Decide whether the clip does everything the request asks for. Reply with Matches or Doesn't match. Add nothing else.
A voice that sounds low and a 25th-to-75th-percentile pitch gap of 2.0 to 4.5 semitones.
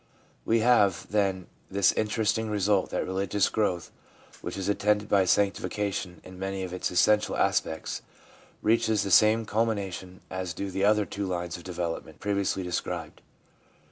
Matches